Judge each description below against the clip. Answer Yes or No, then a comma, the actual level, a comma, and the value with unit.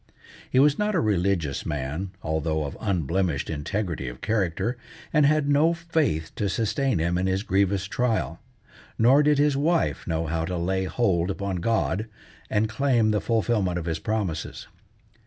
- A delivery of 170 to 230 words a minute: No, average, 160 wpm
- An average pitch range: No, wide, 6.6 semitones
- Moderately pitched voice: No, low, 100 Hz